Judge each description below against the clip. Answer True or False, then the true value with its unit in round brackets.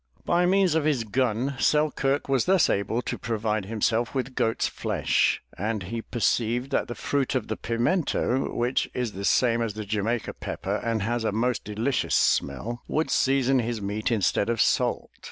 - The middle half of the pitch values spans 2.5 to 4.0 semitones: True (3.5 semitones)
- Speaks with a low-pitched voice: True (120 Hz)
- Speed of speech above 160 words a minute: True (175 wpm)